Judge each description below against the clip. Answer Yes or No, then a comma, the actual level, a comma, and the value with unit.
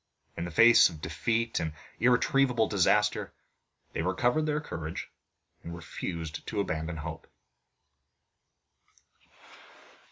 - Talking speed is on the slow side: Yes, slow, 100 wpm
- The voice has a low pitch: Yes, very low, 95 Hz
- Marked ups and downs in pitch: Yes, wide, 6.4 semitones